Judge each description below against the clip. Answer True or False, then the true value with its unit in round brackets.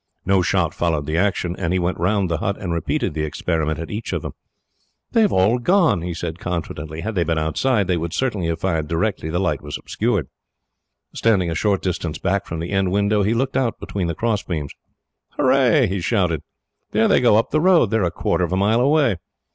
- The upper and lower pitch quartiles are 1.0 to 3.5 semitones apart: False (4.8 semitones)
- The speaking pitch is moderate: False (95 Hz)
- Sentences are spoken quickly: True (220 wpm)